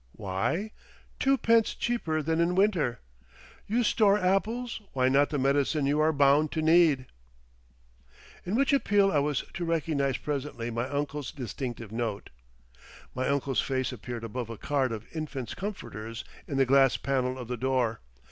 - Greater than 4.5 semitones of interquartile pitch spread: Yes, average, 5.0 semitones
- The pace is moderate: Yes, average, 155 wpm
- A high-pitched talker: No, medium, 140 Hz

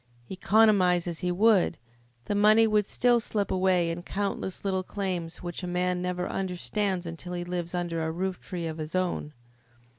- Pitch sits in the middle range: Yes, medium, 180 Hz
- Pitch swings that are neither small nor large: No, narrow, 2.2 semitones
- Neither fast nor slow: Yes, average, 175 wpm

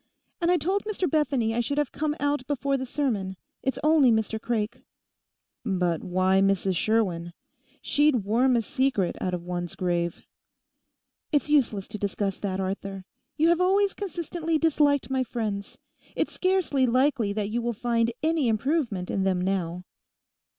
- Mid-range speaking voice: No, high, 235 Hz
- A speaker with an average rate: Yes, average, 160 wpm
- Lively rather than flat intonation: Yes, wide, 7.1 semitones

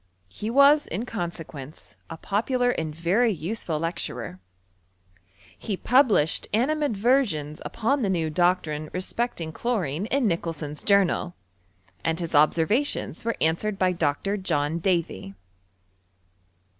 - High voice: No, medium, 180 Hz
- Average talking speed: No, slow, 110 wpm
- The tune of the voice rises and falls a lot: Yes, wide, 6.2 semitones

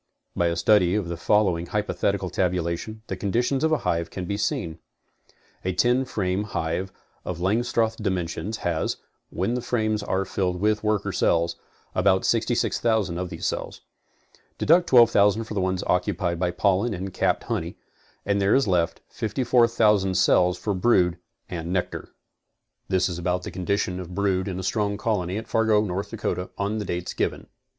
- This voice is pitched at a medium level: No, very low, 95 Hz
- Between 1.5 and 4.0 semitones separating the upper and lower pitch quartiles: Yes, average, 3.2 semitones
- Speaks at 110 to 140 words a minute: No, average, 165 wpm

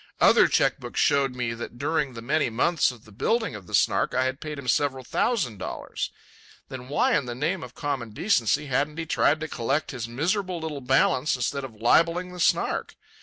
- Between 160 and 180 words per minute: No, fast, 205 wpm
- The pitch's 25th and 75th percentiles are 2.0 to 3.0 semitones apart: No, average, 4.5 semitones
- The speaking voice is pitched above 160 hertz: No, low, 135 Hz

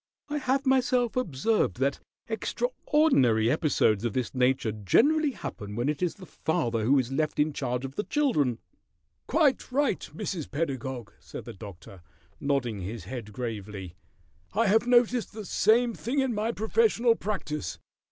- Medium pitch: Yes, medium, 150 Hz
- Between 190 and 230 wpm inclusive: No, average, 150 wpm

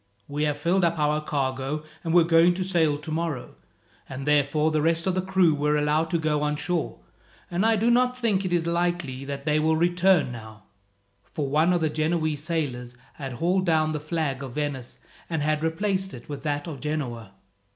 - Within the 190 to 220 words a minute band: Yes, average, 200 wpm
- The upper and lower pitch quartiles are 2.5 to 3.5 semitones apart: Yes, average, 3.0 semitones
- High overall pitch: No, medium, 155 Hz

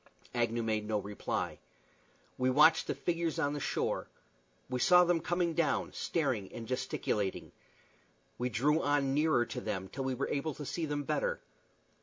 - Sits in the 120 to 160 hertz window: Yes, medium, 140 Hz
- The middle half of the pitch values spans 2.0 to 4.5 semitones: No, average, 5.3 semitones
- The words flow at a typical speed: Yes, average, 165 wpm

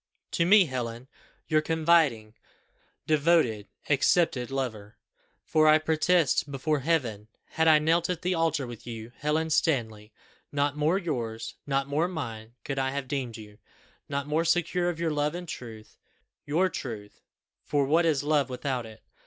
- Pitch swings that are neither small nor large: Yes, average, 5.0 semitones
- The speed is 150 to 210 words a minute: Yes, average, 155 wpm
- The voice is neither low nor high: Yes, medium, 145 Hz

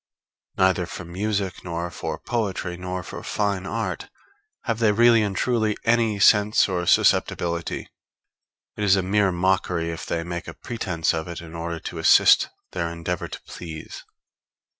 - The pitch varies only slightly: No, average, 3.5 semitones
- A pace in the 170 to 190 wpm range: No, average, 160 wpm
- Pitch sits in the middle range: No, very low, 95 Hz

